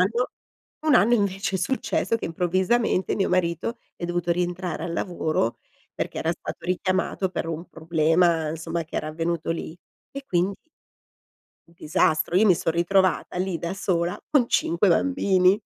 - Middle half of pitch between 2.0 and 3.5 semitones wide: Yes, narrow, 2.4 semitones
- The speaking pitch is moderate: Yes, medium, 175 Hz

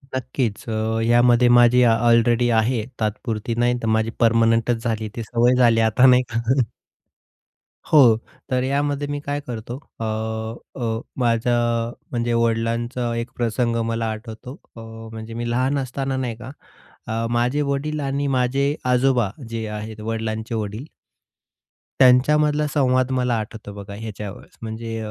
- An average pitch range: No, narrow, 2.1 semitones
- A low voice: Yes, low, 120 Hz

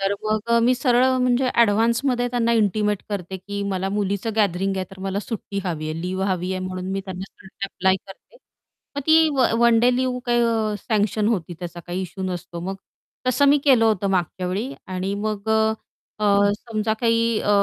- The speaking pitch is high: Yes, high, 205 Hz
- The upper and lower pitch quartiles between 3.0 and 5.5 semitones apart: Yes, average, 3.6 semitones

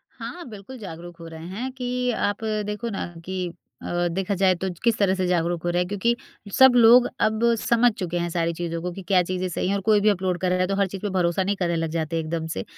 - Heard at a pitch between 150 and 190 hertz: Yes, medium, 185 Hz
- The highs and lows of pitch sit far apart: No, average, 3.2 semitones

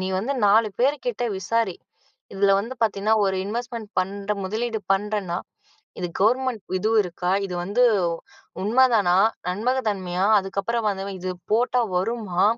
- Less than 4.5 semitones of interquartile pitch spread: Yes, average, 3.3 semitones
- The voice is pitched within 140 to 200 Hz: No, high, 210 Hz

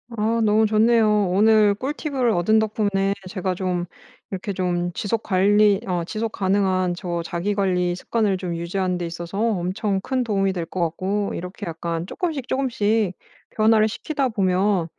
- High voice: Yes, high, 200 Hz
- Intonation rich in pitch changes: No, average, 3.2 semitones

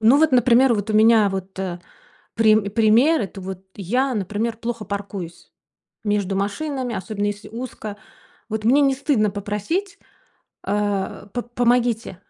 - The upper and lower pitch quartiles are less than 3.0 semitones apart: No, average, 3.3 semitones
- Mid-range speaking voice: No, high, 215 Hz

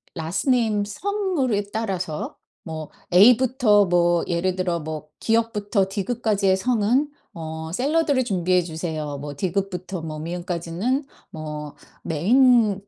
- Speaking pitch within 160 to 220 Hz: Yes, high, 190 Hz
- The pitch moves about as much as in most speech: No, wide, 5.7 semitones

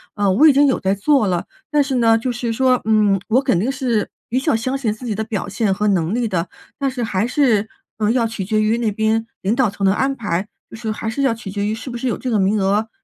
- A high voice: Yes, high, 225 Hz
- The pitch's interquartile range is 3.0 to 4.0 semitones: Yes, average, 3.5 semitones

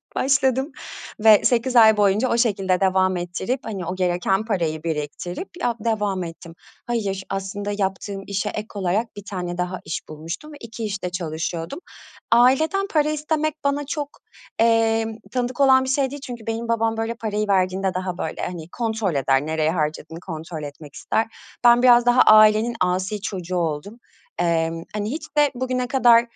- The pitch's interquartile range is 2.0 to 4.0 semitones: No, average, 5.1 semitones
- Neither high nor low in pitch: No, high, 210 Hz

